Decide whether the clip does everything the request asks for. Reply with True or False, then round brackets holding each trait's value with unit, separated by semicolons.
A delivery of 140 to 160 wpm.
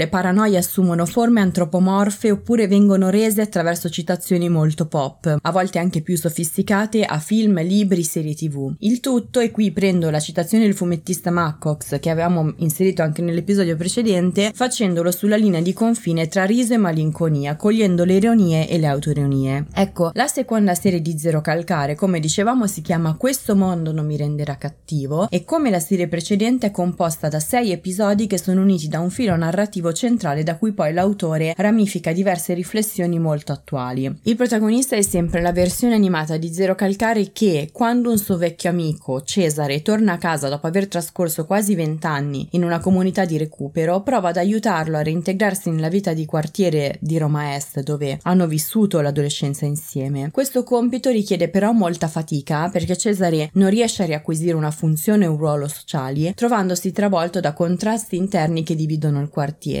False (170 wpm)